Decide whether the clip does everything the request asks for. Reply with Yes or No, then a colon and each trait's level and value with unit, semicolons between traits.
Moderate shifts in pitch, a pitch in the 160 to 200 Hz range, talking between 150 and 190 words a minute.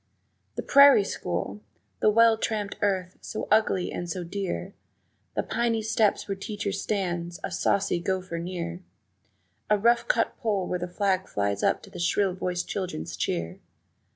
Yes: average, 3.3 semitones; high, 190 Hz; average, 155 wpm